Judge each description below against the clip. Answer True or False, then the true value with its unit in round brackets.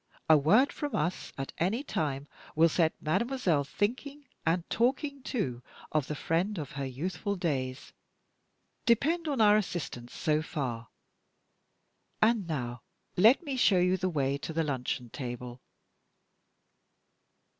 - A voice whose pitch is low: False (165 Hz)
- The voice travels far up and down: True (7.9 semitones)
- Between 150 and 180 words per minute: False (135 wpm)